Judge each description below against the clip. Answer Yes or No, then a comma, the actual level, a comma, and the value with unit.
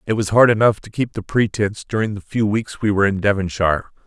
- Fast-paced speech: Yes, fast, 235 wpm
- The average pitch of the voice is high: No, low, 105 Hz